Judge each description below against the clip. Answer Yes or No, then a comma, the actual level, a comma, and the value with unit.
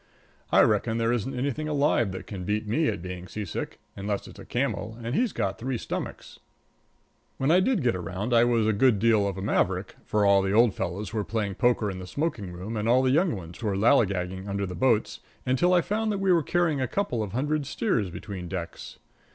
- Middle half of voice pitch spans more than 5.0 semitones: Yes, wide, 5.4 semitones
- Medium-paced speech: No, fast, 220 wpm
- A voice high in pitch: No, low, 110 Hz